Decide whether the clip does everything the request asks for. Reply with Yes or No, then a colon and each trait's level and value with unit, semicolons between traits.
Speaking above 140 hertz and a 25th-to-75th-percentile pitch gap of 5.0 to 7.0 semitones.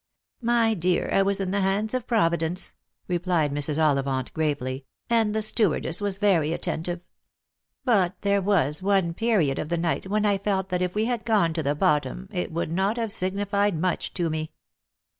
No: medium, 185 Hz; average, 4.1 semitones